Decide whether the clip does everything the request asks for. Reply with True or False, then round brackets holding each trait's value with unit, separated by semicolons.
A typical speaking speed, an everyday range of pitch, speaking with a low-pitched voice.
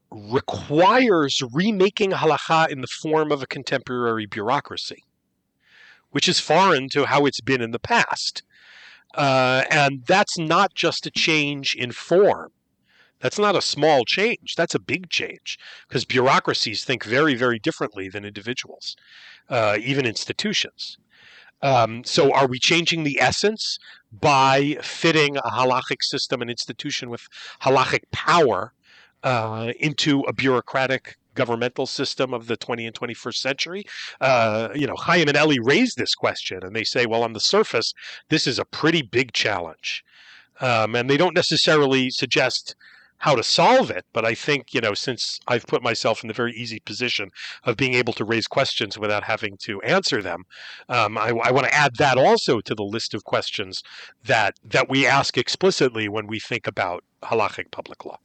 True (165 wpm; 4.6 semitones; 130 Hz)